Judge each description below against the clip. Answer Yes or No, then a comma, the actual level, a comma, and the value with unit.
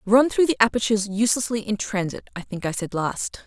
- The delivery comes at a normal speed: No, fast, 210 wpm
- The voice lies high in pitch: Yes, high, 215 Hz